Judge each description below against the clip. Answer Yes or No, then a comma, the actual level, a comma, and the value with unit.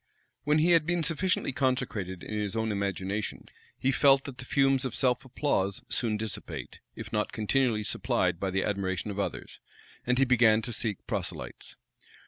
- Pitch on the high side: No, low, 115 Hz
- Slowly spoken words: No, average, 170 wpm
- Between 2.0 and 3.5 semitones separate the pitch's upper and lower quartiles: No, average, 4.8 semitones